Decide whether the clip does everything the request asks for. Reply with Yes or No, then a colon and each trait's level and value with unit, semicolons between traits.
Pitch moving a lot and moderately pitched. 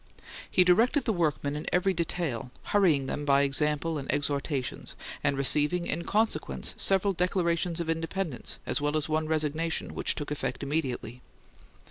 No: average, 3.8 semitones; medium, 155 Hz